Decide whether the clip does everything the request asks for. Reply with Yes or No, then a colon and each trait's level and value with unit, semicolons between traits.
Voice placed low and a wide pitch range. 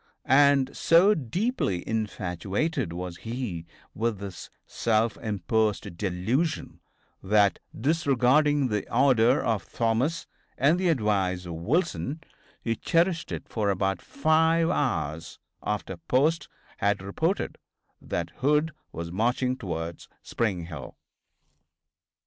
Yes: low, 115 Hz; wide, 7.3 semitones